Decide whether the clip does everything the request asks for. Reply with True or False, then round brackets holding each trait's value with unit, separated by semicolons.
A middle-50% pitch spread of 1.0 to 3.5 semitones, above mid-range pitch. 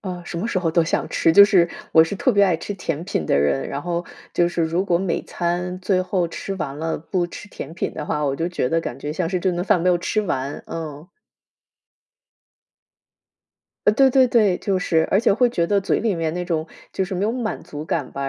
False (3.1 semitones; 175 Hz)